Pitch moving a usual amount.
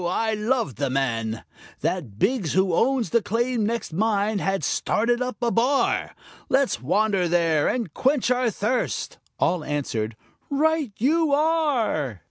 No: wide, 7.6 semitones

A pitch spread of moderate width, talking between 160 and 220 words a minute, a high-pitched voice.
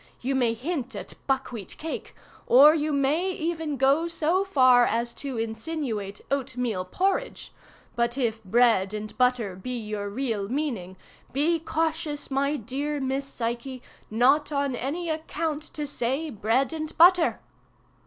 No: average, 4.8 semitones; average, 145 wpm; very high, 270 Hz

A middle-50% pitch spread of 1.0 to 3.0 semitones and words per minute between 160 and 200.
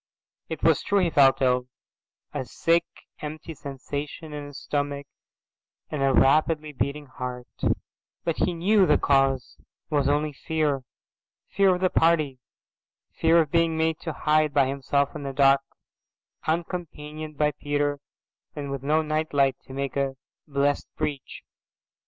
No: narrow, 2.5 semitones; average, 145 wpm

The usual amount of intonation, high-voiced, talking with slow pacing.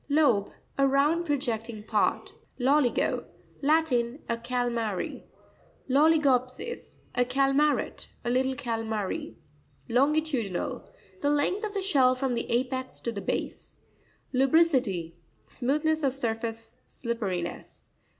Yes: average, 4.1 semitones; very high, 255 Hz; slow, 90 wpm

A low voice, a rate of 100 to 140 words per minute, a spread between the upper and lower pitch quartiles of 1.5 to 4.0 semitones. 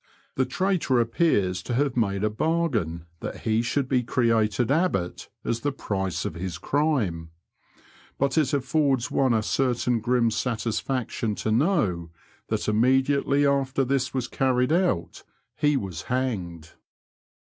No: low, 125 Hz; slow, 135 wpm; average, 4.5 semitones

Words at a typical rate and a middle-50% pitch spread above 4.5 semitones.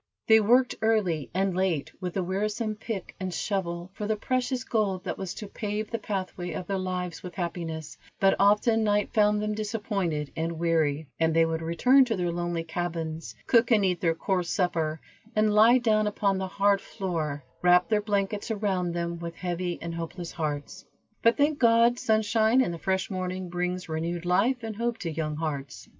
No: average, 185 wpm; average, 4.0 semitones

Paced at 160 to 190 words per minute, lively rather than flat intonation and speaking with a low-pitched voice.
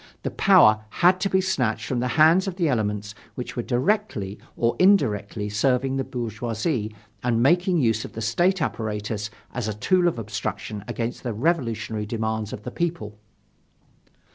Yes: average, 165 wpm; wide, 7.5 semitones; low, 120 Hz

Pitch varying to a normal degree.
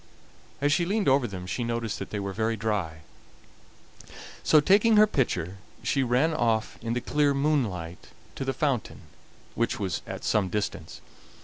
No: wide, 6.2 semitones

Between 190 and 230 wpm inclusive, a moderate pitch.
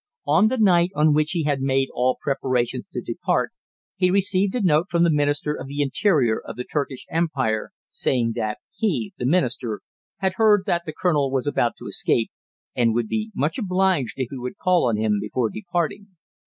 Yes: average, 195 wpm; medium, 150 Hz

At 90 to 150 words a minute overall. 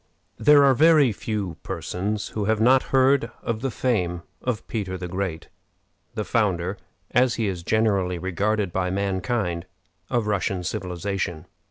Yes: average, 145 wpm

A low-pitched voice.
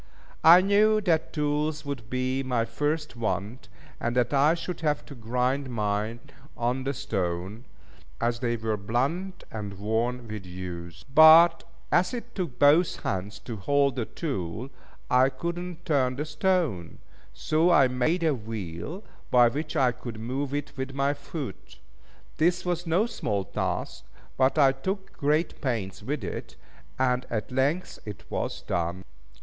Yes: low, 130 Hz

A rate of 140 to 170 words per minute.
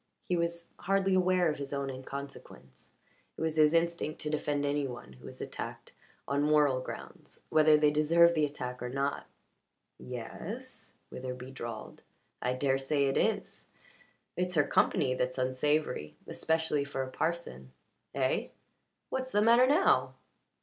Yes: average, 150 wpm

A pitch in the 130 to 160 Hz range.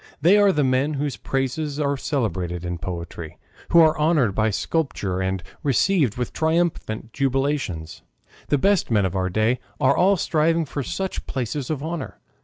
Yes: low, 135 Hz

